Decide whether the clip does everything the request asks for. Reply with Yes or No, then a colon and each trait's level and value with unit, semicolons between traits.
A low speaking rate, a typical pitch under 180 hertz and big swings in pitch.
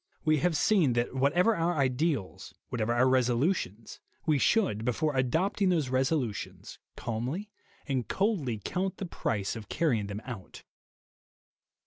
Yes: slow, 130 wpm; low, 135 Hz; wide, 6.2 semitones